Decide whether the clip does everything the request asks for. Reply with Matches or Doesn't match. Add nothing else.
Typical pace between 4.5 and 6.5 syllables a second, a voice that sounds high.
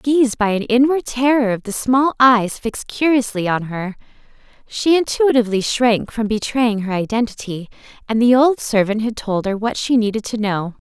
Matches